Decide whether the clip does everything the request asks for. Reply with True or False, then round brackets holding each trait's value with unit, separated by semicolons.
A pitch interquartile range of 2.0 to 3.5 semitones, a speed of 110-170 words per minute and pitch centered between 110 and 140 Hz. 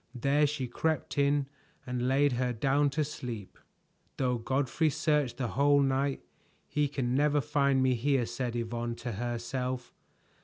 True (2.7 semitones; 150 wpm; 135 Hz)